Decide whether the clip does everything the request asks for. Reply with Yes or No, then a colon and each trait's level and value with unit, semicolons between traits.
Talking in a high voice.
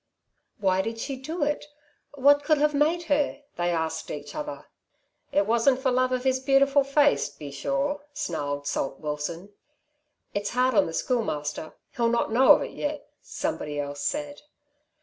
Yes: very high, 250 Hz